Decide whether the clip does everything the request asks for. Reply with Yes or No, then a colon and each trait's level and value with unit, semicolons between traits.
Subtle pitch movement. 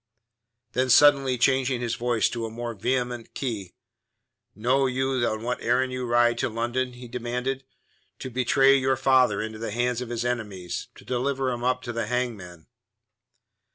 Yes: narrow, 1.7 semitones